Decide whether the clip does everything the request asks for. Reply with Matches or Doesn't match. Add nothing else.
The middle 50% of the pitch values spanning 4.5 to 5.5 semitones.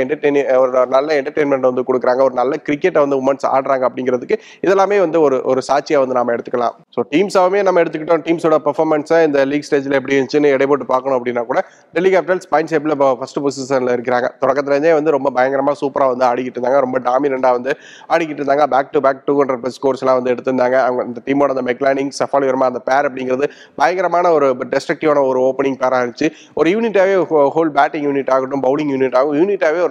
Doesn't match